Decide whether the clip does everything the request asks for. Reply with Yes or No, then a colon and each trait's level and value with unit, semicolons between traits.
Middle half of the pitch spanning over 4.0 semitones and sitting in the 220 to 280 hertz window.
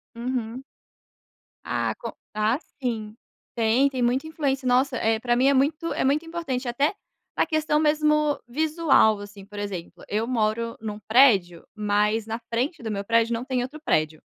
Yes: average, 4.4 semitones; high, 240 Hz